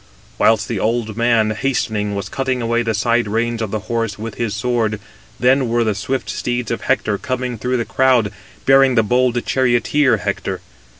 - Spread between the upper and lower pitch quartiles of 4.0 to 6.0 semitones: No, narrow, 2.5 semitones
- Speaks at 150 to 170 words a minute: No, average, 180 wpm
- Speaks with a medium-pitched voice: No, low, 120 Hz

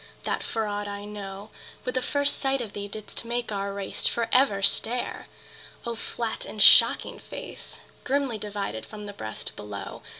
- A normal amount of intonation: Yes, average, 3.1 semitones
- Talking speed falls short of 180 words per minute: Yes, average, 170 wpm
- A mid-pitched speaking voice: No, high, 210 Hz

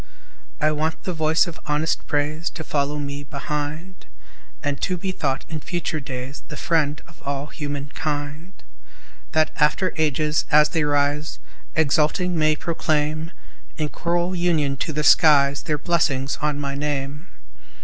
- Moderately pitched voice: Yes, medium, 150 Hz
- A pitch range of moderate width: No, narrow, 1.8 semitones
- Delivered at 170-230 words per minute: No, average, 145 wpm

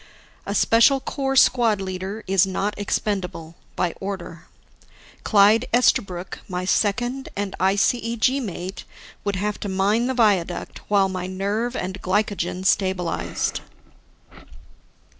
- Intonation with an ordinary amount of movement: Yes, average, 3.1 semitones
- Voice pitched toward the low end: No, high, 200 Hz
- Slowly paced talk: Yes, slow, 115 wpm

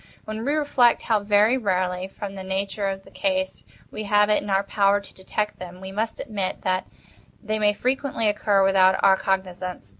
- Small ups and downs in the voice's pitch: Yes, narrow, 2.2 semitones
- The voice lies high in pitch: Yes, high, 200 Hz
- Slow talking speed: No, average, 190 wpm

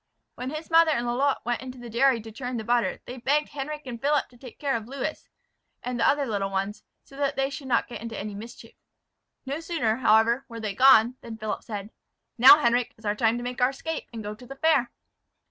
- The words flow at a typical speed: No, fast, 230 wpm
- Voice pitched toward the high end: Yes, high, 245 Hz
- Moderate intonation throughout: Yes, average, 3.3 semitones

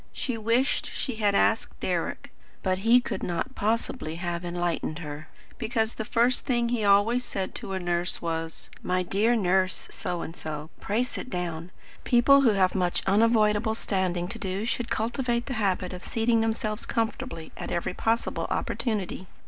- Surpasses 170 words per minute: No, average, 165 wpm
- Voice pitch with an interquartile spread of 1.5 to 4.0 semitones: No, average, 4.5 semitones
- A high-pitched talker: Yes, high, 205 Hz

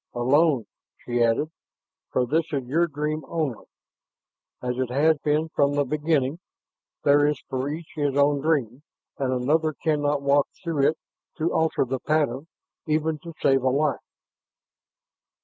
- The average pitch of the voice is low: No, medium, 145 Hz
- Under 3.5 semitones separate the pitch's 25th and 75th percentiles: Yes, average, 2.8 semitones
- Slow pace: No, average, 150 wpm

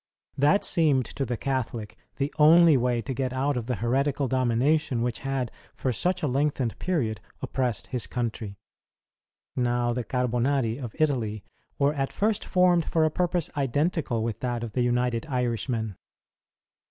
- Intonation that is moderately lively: Yes, average, 3.5 semitones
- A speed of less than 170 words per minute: Yes, average, 155 wpm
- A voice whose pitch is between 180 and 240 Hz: No, low, 130 Hz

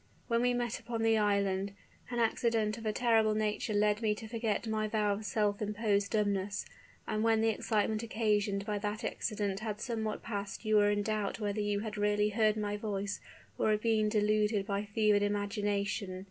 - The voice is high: Yes, high, 210 Hz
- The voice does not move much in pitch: Yes, narrow, 1.3 semitones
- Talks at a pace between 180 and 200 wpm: Yes, average, 190 wpm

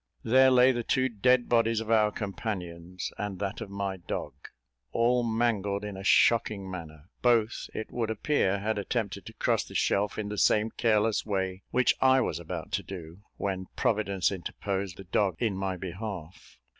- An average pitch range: Yes, average, 3.2 semitones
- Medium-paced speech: Yes, average, 175 wpm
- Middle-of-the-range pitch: No, low, 105 Hz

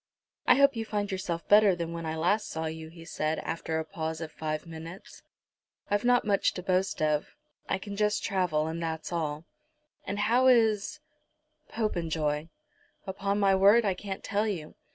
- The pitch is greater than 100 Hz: Yes, medium, 185 Hz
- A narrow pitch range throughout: No, average, 4.4 semitones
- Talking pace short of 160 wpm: No, average, 175 wpm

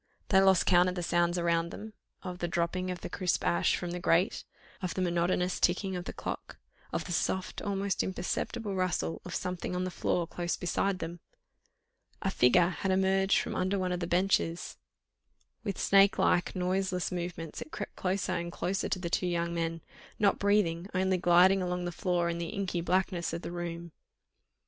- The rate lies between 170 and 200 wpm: Yes, average, 185 wpm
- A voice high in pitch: No, medium, 180 Hz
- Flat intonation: Yes, narrow, 1.7 semitones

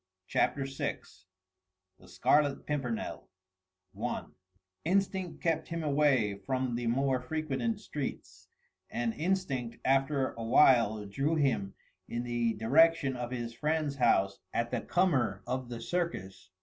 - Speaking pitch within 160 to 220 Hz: No, low, 130 Hz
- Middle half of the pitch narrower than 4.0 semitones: No, average, 4.6 semitones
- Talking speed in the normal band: No, slow, 125 wpm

